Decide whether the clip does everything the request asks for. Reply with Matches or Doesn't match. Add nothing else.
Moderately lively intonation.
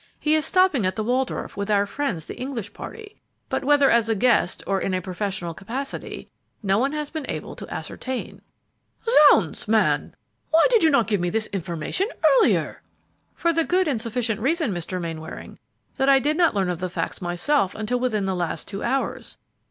Doesn't match